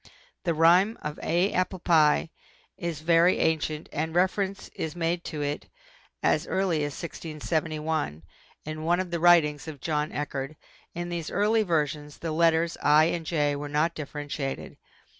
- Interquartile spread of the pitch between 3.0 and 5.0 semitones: No, narrow, 2.5 semitones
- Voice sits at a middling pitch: Yes, medium, 160 Hz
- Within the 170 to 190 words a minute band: No, average, 155 wpm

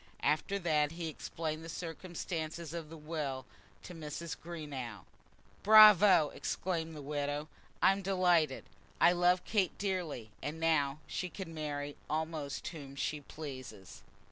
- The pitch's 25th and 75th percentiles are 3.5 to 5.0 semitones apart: No, average, 3.0 semitones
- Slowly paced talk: Yes, slow, 130 wpm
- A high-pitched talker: No, medium, 160 Hz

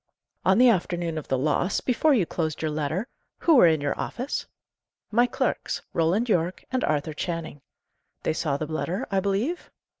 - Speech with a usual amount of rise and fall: No, wide, 6.4 semitones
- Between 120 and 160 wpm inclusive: No, average, 175 wpm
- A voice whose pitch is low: No, medium, 175 Hz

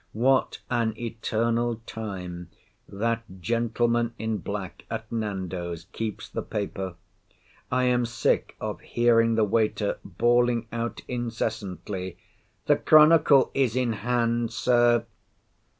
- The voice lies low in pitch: Yes, low, 115 Hz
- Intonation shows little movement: Yes, narrow, 2.3 semitones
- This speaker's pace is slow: Yes, slow, 110 wpm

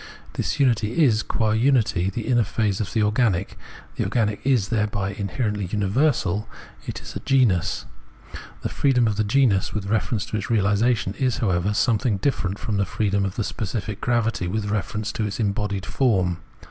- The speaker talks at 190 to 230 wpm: No, average, 165 wpm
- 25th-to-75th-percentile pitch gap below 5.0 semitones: Yes, average, 2.9 semitones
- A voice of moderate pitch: No, low, 105 Hz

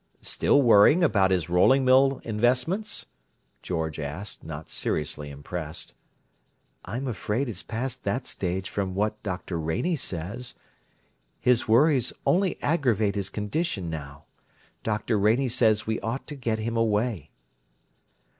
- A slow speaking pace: Yes, slow, 125 wpm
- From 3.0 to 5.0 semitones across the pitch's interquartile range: No, wide, 5.5 semitones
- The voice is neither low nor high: No, low, 110 Hz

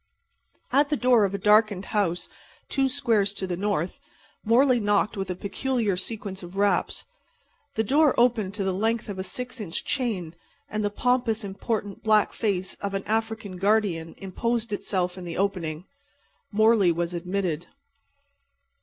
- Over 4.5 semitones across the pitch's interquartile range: No, average, 3.2 semitones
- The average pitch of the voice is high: Yes, high, 205 Hz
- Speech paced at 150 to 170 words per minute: Yes, average, 155 wpm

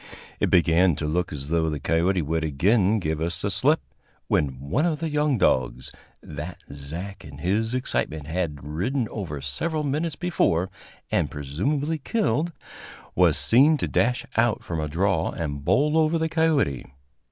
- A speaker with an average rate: Yes, average, 165 wpm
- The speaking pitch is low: Yes, very low, 90 Hz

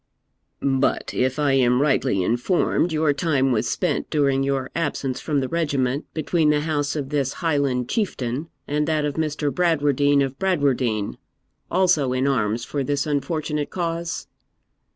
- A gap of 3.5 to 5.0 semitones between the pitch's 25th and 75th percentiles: No, average, 2.9 semitones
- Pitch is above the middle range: No, medium, 145 Hz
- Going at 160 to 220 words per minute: No, average, 150 wpm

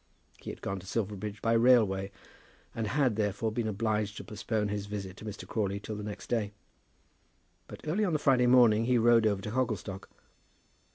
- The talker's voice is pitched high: No, low, 110 Hz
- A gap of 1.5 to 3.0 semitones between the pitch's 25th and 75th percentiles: Yes, narrow, 2.5 semitones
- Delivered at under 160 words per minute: No, average, 185 wpm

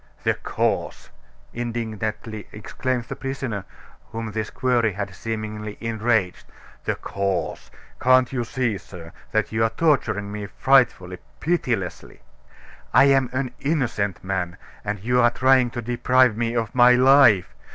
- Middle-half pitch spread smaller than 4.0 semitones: Yes, average, 3.5 semitones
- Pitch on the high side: No, low, 115 Hz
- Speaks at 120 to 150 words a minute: Yes, slow, 135 wpm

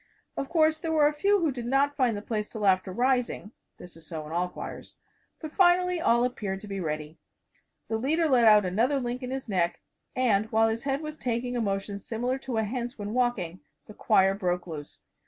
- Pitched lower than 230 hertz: No, high, 235 Hz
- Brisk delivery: Yes, fast, 215 wpm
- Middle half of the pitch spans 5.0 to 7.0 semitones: Yes, wide, 5.5 semitones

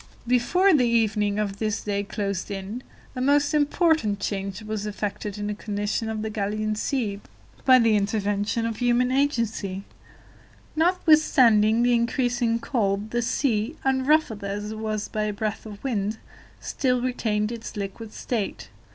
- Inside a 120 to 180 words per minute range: Yes, average, 150 wpm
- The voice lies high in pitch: Yes, high, 220 Hz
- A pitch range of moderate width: Yes, average, 3.2 semitones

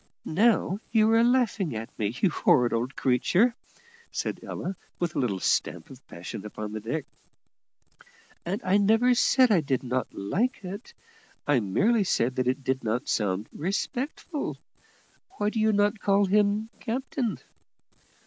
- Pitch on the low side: No, high, 190 Hz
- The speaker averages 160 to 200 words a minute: No, average, 150 wpm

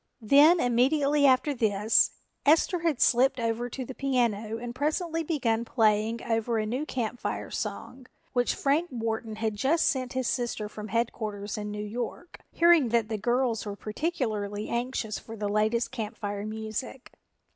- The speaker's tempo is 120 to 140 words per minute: No, average, 160 wpm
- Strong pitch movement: No, average, 3.5 semitones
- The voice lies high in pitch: Yes, high, 235 Hz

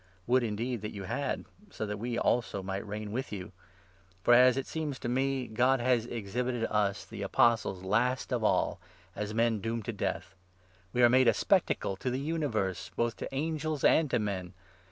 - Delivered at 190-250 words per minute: Yes, average, 195 wpm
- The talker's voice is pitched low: Yes, low, 120 Hz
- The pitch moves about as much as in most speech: Yes, average, 3.5 semitones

